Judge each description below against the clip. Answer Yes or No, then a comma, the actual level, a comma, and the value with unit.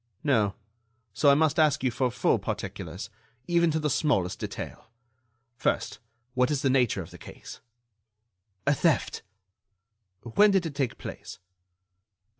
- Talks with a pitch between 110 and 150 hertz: Yes, medium, 140 Hz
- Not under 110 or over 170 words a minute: Yes, average, 140 wpm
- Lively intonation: No, average, 4.6 semitones